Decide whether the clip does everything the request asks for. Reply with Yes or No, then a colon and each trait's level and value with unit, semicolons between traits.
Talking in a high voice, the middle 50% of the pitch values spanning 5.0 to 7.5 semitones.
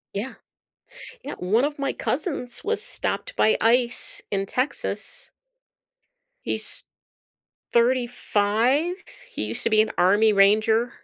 No: high, 235 Hz; average, 3.7 semitones